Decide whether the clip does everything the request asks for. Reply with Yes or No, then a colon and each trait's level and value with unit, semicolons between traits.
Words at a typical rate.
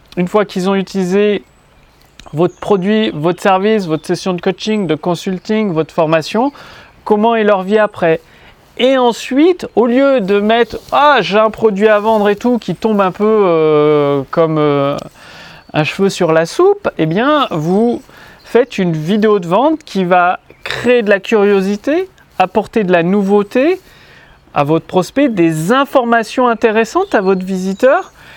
Yes: average, 160 wpm